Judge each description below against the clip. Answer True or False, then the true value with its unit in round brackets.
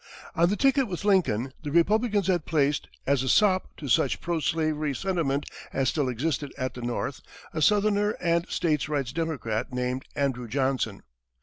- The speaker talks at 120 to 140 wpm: False (170 wpm)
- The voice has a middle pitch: True (150 Hz)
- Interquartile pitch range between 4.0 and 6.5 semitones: True (5.1 semitones)